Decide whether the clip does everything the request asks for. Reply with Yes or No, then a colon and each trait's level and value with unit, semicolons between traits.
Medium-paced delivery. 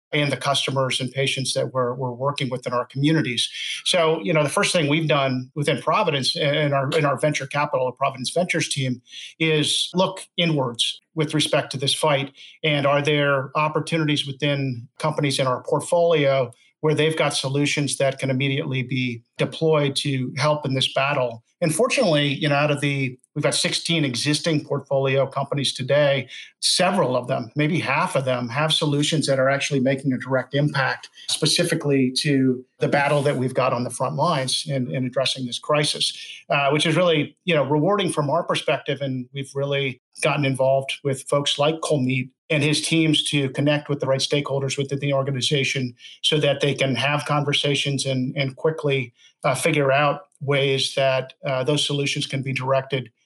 Yes: average, 180 wpm